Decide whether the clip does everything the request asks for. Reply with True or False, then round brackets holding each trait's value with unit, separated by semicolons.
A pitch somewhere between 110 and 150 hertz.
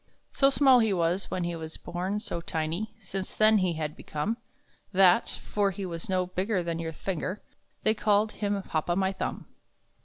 False (190 Hz)